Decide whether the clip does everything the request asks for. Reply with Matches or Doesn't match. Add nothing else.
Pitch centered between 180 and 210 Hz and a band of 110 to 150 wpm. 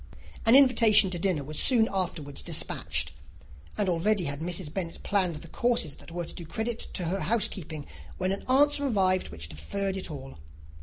Doesn't match